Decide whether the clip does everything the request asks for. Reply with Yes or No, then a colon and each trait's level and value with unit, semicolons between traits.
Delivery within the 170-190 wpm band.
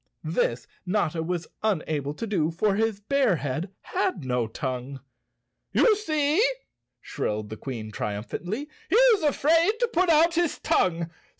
No: average, 140 wpm